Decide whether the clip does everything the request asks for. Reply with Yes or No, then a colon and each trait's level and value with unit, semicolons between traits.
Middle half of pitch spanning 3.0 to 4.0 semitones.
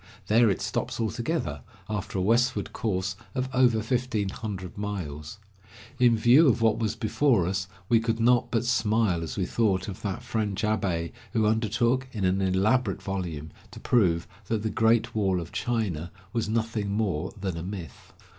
Yes: average, 3.6 semitones